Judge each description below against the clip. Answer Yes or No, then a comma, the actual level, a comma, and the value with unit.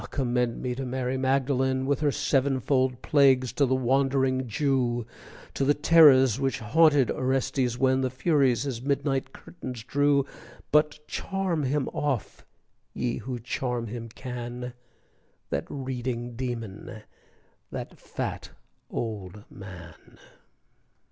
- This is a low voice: Yes, low, 130 Hz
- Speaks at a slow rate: Yes, slow, 120 wpm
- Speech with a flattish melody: Yes, narrow, 2.1 semitones